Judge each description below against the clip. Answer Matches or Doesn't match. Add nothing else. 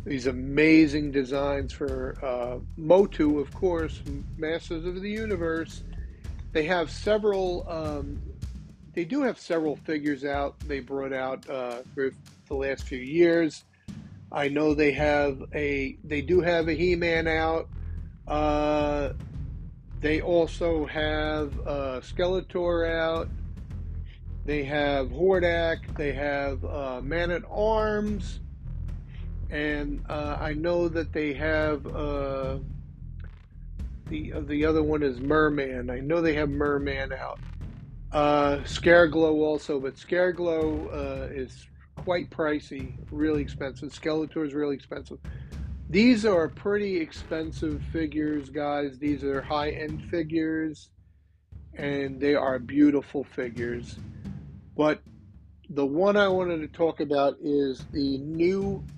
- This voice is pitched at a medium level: Matches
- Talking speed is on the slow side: Matches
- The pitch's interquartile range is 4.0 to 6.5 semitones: Doesn't match